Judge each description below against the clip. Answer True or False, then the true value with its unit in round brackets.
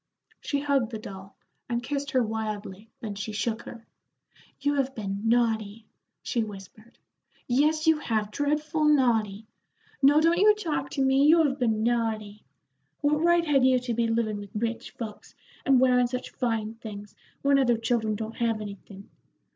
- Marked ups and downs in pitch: False (4.3 semitones)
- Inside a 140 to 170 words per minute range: True (165 wpm)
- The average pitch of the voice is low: False (235 Hz)